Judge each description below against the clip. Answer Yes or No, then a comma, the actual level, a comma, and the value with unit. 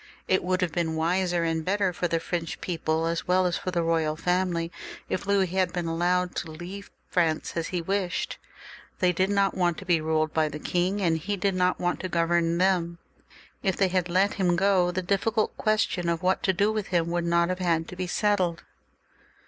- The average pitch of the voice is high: No, medium, 180 Hz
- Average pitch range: No, narrow, 2.0 semitones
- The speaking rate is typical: No, fast, 215 wpm